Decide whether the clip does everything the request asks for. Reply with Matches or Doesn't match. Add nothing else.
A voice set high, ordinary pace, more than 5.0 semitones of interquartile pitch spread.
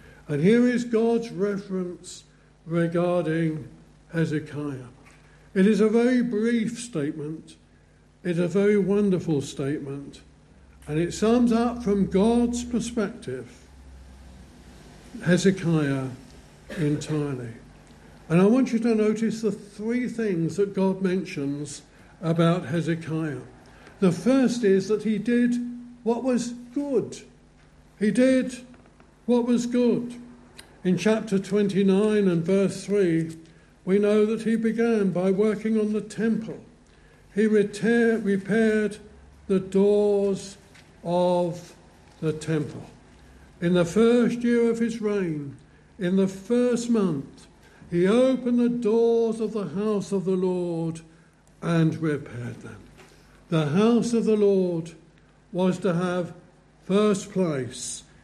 Doesn't match